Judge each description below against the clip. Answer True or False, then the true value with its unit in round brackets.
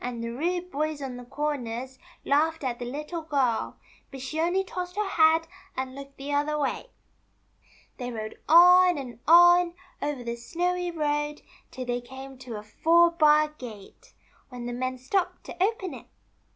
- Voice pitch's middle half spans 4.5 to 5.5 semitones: True (5.2 semitones)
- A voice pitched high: True (290 Hz)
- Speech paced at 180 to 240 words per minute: False (165 wpm)